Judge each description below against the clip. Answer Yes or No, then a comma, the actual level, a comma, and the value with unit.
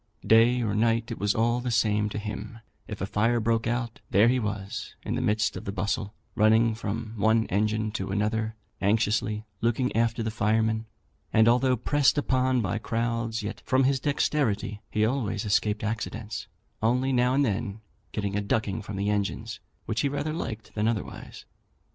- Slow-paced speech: No, average, 180 wpm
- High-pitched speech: No, low, 110 Hz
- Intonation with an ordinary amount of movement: No, narrow, 2.0 semitones